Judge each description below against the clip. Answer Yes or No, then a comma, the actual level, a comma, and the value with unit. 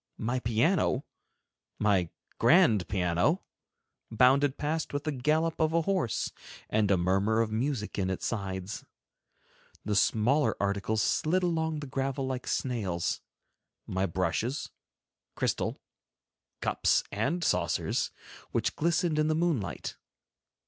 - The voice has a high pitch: No, low, 125 Hz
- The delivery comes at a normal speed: No, slow, 120 wpm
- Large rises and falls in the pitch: Yes, wide, 7.4 semitones